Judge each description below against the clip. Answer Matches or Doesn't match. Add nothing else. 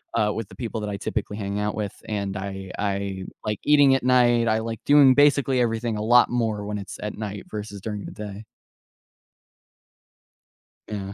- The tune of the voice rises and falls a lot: Doesn't match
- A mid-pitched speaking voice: Doesn't match